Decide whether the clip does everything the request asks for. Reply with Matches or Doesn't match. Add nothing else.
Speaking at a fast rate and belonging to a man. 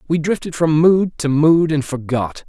Doesn't match